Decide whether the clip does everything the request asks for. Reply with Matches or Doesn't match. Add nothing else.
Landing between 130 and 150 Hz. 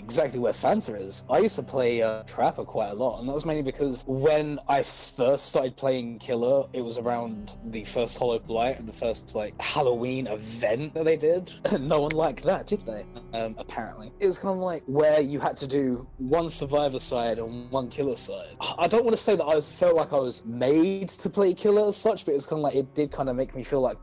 Matches